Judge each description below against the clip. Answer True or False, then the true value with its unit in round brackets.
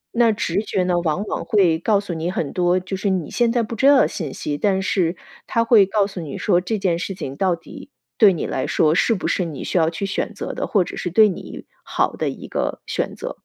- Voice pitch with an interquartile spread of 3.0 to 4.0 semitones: True (3.5 semitones)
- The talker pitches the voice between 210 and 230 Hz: False (185 Hz)